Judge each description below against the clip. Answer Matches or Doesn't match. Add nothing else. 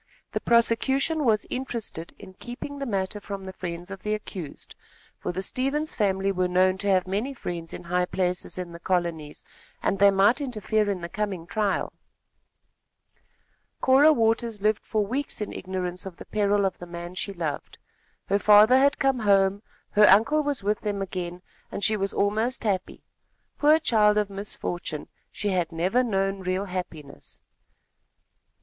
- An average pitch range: Matches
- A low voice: Doesn't match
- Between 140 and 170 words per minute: Matches